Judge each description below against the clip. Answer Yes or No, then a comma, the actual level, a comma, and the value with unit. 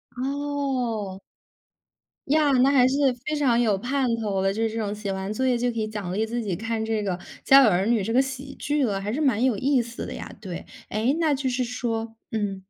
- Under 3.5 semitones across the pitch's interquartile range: No, average, 4.1 semitones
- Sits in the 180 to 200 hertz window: No, high, 235 Hz